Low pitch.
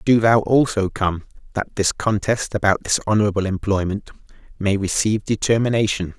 Yes: low, 105 Hz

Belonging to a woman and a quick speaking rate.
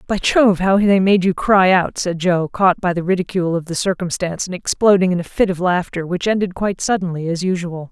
Yes: female; fast, 225 wpm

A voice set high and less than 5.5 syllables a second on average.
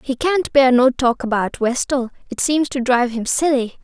Yes: very high, 260 Hz; 4.8 syllables/s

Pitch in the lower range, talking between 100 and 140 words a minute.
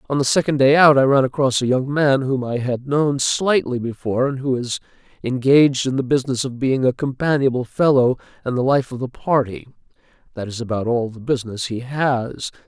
No: low, 130 Hz; fast, 205 wpm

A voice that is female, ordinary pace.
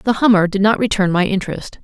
No: female; fast, 230 wpm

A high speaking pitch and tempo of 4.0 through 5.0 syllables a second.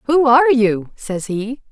Yes: high, 240 Hz; 4.1 syllables/s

